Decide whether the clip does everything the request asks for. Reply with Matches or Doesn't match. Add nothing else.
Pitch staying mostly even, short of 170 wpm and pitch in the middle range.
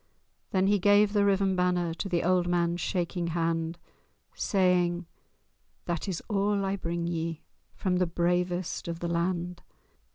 Matches